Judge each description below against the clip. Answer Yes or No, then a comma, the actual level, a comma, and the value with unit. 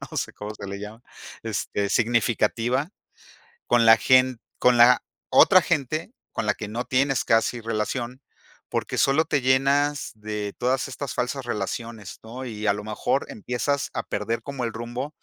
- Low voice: Yes, low, 120 Hz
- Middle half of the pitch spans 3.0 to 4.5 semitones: Yes, average, 3.4 semitones